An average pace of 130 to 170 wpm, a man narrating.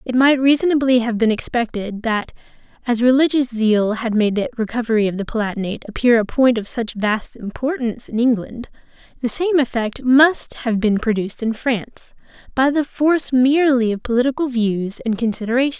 No: average, 165 wpm; female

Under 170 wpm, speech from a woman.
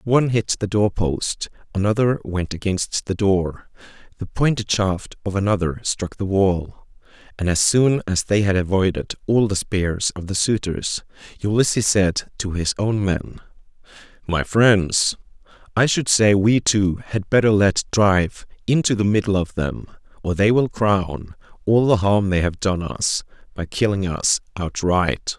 No: average, 160 wpm; male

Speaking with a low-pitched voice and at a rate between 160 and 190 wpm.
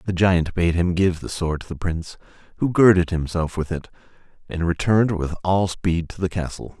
No: very low, 85 Hz; fast, 205 wpm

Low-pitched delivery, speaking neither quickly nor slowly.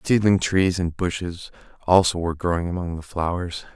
Yes: very low, 90 Hz; average, 160 wpm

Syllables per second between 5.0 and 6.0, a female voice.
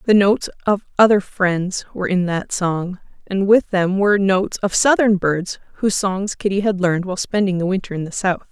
Yes: 5.5 syllables/s; female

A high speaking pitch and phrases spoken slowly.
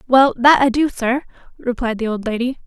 No: very high, 250 Hz; fast, 205 wpm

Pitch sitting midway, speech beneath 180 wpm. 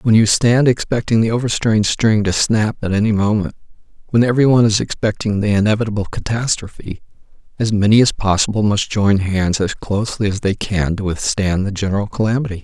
No: low, 105 Hz; average, 170 wpm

